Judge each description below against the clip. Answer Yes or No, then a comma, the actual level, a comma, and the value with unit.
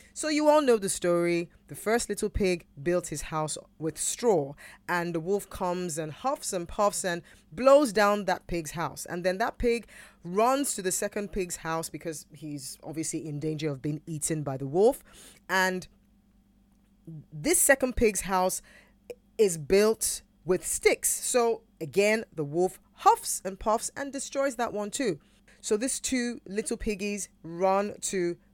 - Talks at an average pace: Yes, average, 165 wpm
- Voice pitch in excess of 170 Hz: Yes, high, 190 Hz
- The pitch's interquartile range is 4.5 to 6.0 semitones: Yes, average, 5.2 semitones